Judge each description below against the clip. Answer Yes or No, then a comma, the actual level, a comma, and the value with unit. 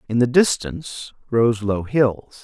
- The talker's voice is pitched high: No, low, 115 Hz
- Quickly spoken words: No, average, 150 wpm